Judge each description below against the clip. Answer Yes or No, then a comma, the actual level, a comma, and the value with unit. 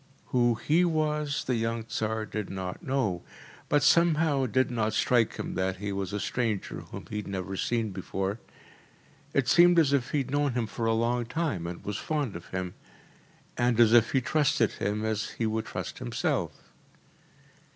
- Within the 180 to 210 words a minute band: Yes, average, 185 wpm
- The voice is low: Yes, low, 115 Hz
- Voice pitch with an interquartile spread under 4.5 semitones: No, average, 5.1 semitones